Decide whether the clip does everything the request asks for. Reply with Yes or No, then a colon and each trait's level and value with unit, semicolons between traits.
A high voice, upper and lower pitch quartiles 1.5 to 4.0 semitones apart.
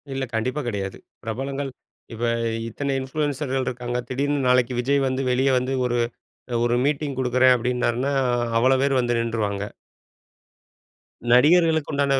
No: low, 130 Hz; narrow, 2.5 semitones